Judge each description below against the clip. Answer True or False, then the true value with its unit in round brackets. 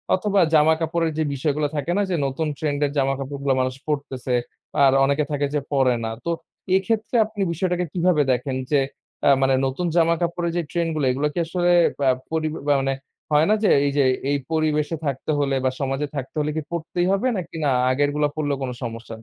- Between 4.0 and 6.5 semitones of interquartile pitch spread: False (3.6 semitones)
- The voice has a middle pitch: True (150 Hz)